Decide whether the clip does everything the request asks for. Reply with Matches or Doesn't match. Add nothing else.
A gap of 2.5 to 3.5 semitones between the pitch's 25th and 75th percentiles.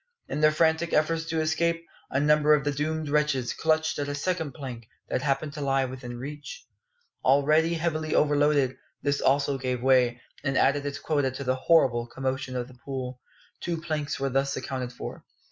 Matches